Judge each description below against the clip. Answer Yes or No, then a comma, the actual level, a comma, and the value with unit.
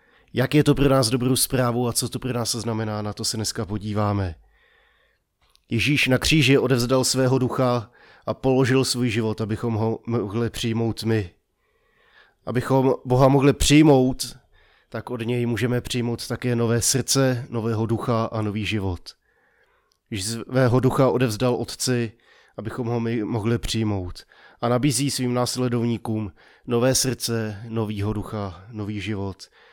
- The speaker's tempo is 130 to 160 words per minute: Yes, average, 140 wpm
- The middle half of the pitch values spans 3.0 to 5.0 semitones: No, narrow, 2.6 semitones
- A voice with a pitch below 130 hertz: Yes, low, 120 Hz